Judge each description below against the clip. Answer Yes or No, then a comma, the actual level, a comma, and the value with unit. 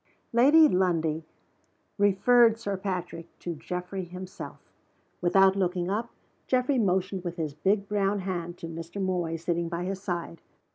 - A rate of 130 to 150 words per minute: Yes, average, 140 wpm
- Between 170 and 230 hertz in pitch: Yes, medium, 185 Hz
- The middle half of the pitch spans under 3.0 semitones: Yes, narrow, 2.6 semitones